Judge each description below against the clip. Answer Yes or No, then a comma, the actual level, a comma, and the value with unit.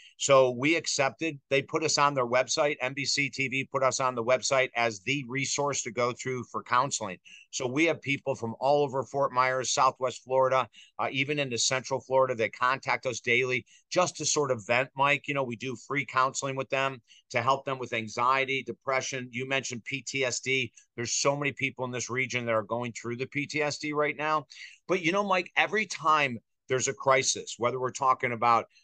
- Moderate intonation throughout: No, narrow, 2.1 semitones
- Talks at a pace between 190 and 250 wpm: Yes, average, 200 wpm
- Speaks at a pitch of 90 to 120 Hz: No, low, 130 Hz